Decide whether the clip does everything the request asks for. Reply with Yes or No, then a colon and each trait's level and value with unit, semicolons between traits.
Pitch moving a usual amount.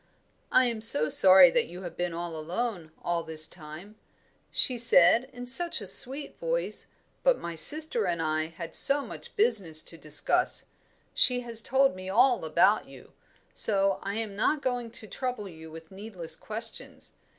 No: wide, 6.7 semitones